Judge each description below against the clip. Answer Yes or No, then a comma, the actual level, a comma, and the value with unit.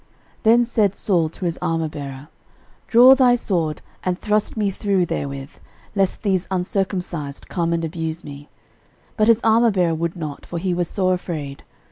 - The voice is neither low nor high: Yes, medium, 180 Hz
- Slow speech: No, average, 160 wpm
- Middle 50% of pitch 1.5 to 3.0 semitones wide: No, average, 4.2 semitones